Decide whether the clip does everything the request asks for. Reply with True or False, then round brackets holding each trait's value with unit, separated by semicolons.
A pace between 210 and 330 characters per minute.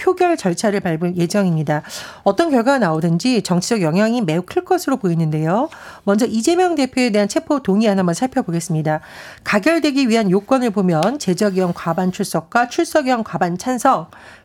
False (375 characters per minute)